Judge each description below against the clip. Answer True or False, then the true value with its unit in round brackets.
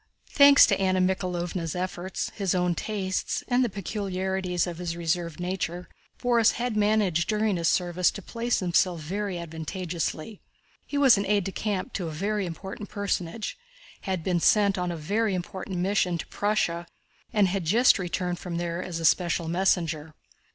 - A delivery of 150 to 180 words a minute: True (165 wpm)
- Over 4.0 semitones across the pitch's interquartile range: False (2.9 semitones)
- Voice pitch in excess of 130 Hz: True (185 Hz)